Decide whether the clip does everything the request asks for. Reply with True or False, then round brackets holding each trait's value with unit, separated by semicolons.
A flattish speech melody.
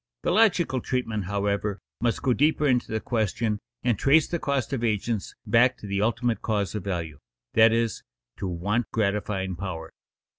False (3.6 semitones)